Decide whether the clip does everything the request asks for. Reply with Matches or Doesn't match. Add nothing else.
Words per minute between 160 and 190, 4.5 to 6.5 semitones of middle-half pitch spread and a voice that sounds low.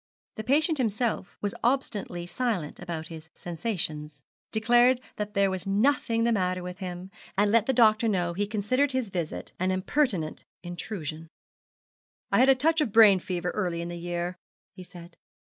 Doesn't match